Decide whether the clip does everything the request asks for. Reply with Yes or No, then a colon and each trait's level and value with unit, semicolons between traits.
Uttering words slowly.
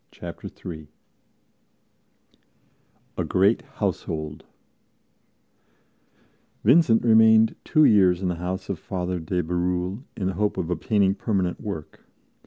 Yes: slow, 110 wpm